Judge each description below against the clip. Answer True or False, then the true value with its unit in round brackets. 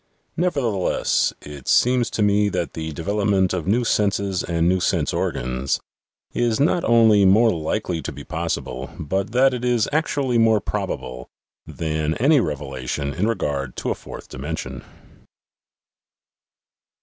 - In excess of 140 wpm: False (135 wpm)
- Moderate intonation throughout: False (6.8 semitones)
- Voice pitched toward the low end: True (100 Hz)